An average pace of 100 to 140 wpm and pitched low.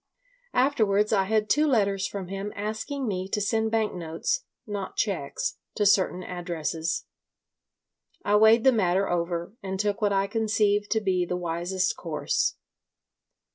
No: slow, 135 wpm; high, 200 Hz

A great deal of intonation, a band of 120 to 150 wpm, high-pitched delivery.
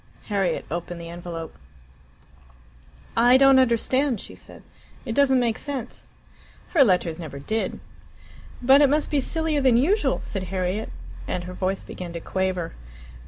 Yes: wide, 6.9 semitones; average, 145 wpm; high, 220 Hz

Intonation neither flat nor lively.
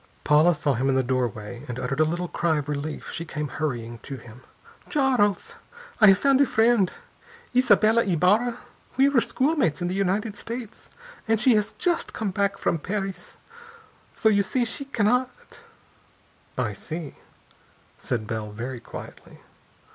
No: wide, 8.3 semitones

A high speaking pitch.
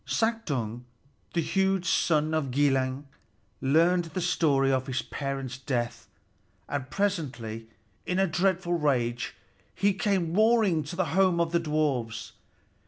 No: medium, 155 Hz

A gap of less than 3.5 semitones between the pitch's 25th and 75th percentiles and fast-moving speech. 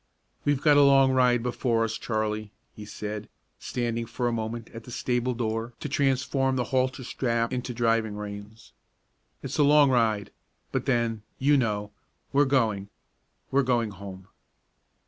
No: average, 3.1 semitones; average, 155 wpm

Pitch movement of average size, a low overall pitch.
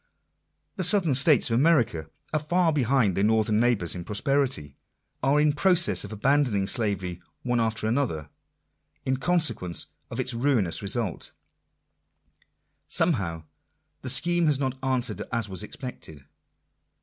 No: wide, 6.0 semitones; low, 125 Hz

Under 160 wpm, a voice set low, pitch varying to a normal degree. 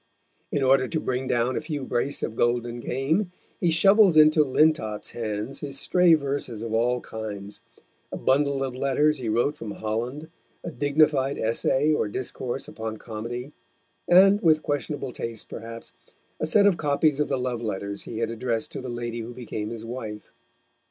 No: average, 170 wpm; low, 130 Hz; average, 4.4 semitones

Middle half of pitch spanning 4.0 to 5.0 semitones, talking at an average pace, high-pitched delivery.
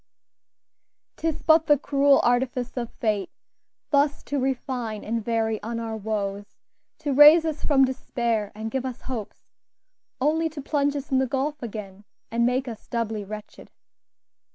Yes: average, 4.3 semitones; average, 155 wpm; very high, 250 Hz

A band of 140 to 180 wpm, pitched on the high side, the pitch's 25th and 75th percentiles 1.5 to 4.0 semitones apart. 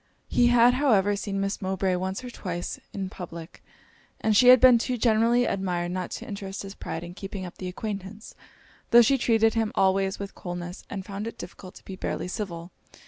No: average, 195 wpm; high, 195 Hz; average, 3.4 semitones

